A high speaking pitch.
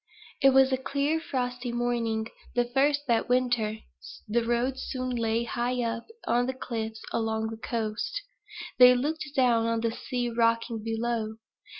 Yes: high, 240 Hz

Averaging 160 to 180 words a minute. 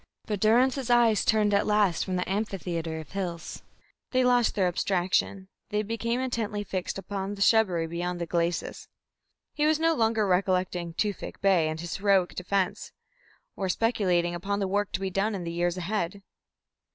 Yes: average, 170 wpm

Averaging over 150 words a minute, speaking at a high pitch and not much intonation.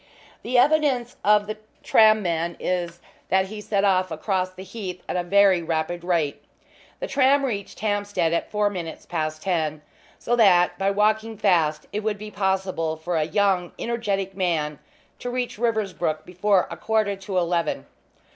No: average, 165 wpm; high, 195 Hz; average, 3.6 semitones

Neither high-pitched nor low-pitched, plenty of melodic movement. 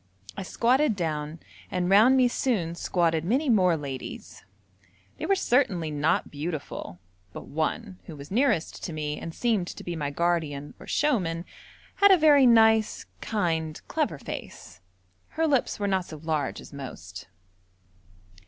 Yes: medium, 175 Hz; wide, 6.9 semitones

